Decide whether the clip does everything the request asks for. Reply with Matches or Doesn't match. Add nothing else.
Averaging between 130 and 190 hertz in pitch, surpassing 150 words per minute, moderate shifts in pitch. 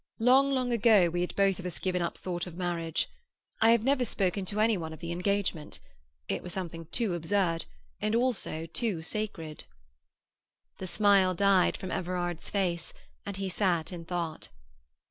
Matches